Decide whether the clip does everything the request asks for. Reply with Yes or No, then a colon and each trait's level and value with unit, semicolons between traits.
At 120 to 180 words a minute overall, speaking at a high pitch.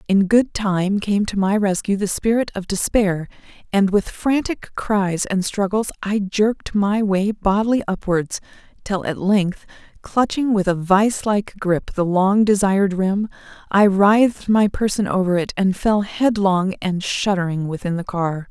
Yes: average, 160 wpm; high, 200 Hz